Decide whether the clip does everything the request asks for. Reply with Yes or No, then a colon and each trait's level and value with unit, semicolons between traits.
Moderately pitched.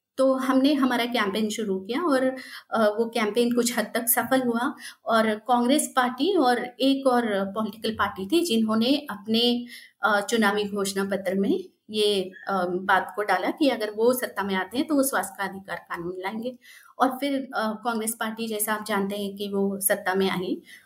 No: high, 225 Hz